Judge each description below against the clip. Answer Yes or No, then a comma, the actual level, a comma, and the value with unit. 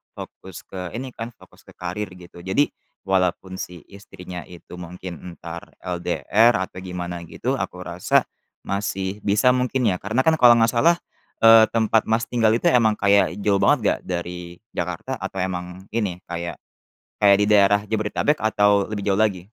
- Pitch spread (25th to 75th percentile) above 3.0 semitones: Yes, average, 3.7 semitones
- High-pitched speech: No, low, 100 Hz